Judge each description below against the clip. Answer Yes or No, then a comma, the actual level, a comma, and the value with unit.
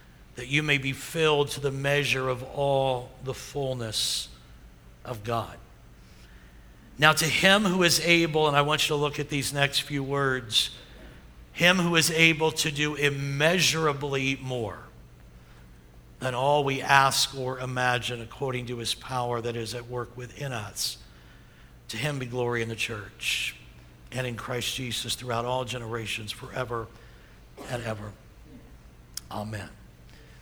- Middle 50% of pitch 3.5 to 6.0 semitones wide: Yes, average, 5.2 semitones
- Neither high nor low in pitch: No, low, 125 Hz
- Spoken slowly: No, average, 145 wpm